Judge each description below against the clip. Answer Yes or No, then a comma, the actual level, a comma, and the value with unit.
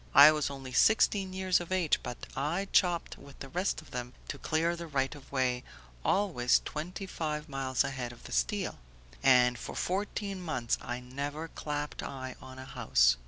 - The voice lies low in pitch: No, medium, 145 Hz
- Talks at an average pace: Yes, average, 180 wpm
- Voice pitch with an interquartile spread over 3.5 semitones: Yes, average, 5.1 semitones